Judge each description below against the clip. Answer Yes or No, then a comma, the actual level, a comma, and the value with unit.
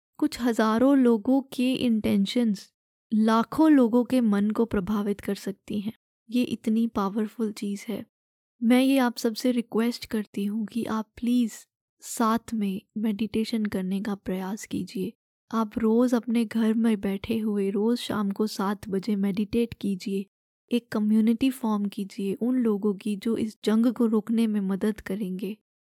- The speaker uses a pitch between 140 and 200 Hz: No, high, 220 Hz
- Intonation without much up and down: Yes, narrow, 2.3 semitones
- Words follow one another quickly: No, average, 150 wpm